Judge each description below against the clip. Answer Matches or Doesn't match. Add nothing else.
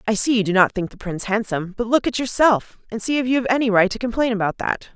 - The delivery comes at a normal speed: Doesn't match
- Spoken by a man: Doesn't match